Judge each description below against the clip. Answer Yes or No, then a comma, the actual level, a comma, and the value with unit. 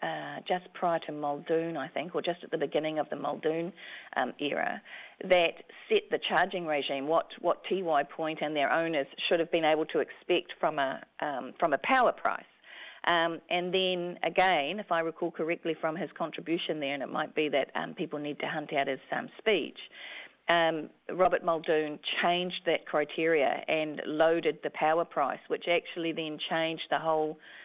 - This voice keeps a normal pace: Yes, average, 185 wpm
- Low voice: No, medium, 165 Hz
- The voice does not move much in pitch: Yes, narrow, 2.1 semitones